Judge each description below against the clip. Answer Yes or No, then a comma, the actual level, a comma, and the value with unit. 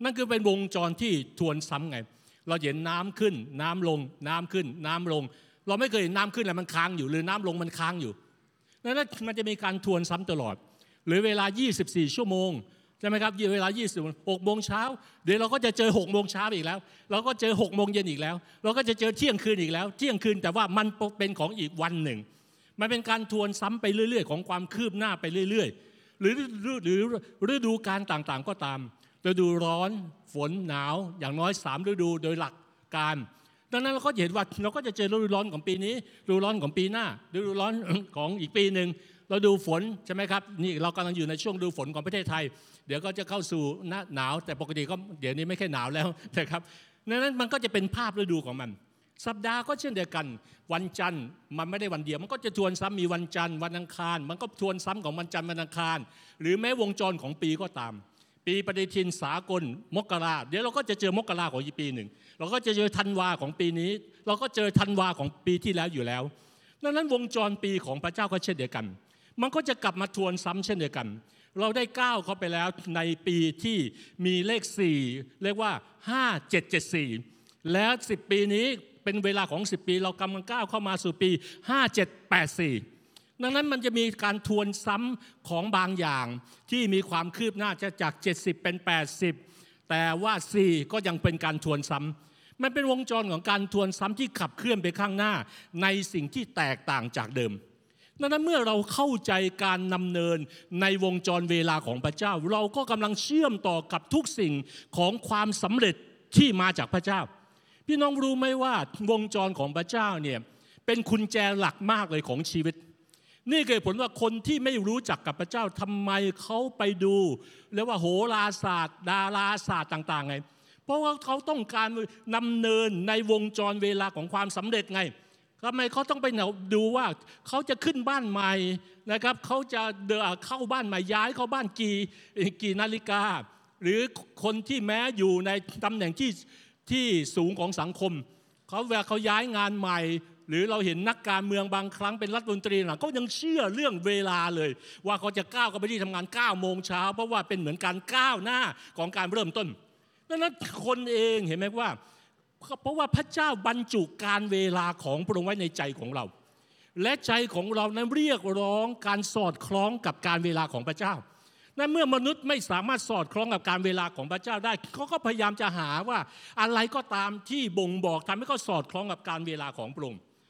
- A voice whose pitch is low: No, high, 195 Hz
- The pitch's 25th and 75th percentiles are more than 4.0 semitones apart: Yes, average, 4.5 semitones